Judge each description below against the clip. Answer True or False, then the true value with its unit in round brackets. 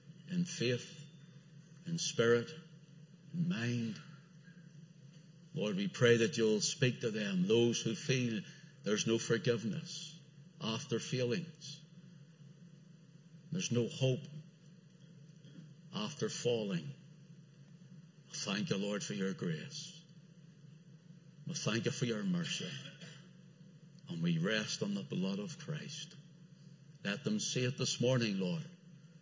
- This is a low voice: False (160 Hz)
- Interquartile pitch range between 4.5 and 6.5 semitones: False (2.6 semitones)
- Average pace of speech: False (115 wpm)